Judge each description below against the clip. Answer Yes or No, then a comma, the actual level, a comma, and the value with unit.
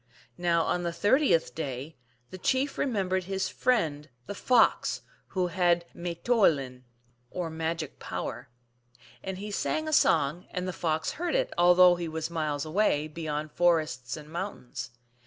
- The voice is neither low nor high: Yes, medium, 175 Hz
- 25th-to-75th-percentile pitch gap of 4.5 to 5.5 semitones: No, average, 3.6 semitones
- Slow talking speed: No, average, 160 wpm